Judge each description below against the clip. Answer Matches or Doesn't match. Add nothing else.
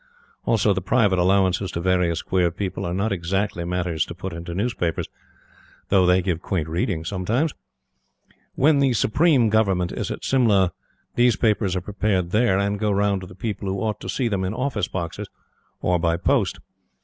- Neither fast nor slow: Matches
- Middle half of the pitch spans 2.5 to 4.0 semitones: Matches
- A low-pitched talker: Matches